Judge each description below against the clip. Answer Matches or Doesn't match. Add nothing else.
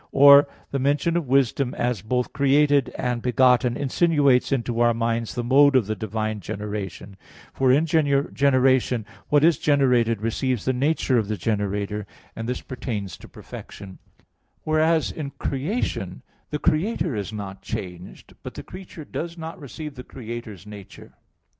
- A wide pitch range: Doesn't match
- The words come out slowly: Doesn't match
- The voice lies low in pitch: Matches